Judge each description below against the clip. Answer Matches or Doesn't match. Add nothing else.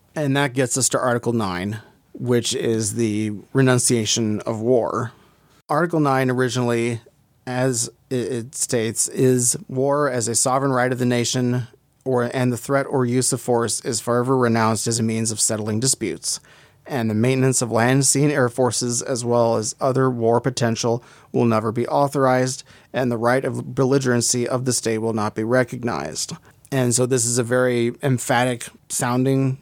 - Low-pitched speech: Matches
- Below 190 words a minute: Matches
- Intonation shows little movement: Matches